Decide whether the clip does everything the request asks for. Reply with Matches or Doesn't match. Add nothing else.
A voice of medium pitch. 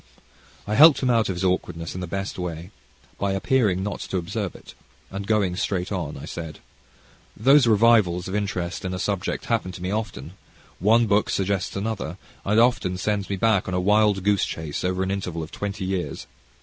Doesn't match